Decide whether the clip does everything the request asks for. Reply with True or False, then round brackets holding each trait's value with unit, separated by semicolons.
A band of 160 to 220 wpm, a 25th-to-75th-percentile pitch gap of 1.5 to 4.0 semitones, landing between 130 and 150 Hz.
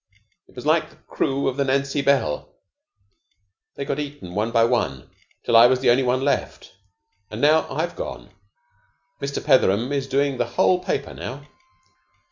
True (165 wpm; 2.9 semitones; 135 Hz)